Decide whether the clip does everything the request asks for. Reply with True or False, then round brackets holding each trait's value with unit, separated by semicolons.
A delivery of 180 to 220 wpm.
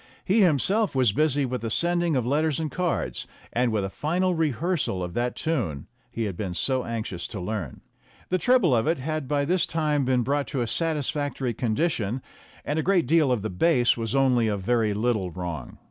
True (200 wpm)